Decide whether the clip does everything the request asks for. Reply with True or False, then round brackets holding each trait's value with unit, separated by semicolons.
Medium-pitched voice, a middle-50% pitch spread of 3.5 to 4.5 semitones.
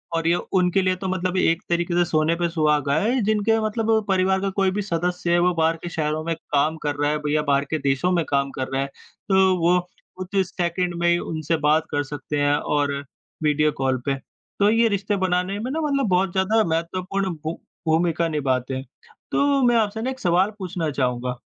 True (175 Hz; 4.1 semitones)